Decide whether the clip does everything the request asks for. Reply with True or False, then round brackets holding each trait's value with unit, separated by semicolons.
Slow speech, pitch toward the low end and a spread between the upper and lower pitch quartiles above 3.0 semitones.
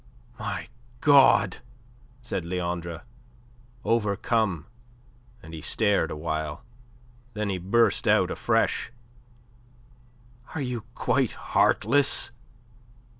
True (80 wpm; 100 Hz; 5.4 semitones)